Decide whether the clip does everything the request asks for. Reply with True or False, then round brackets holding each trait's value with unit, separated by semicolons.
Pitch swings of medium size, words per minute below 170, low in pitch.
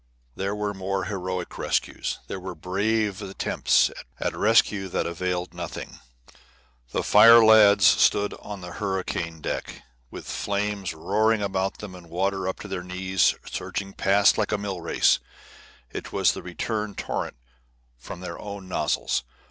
False (2.1 semitones; 150 wpm; 95 Hz)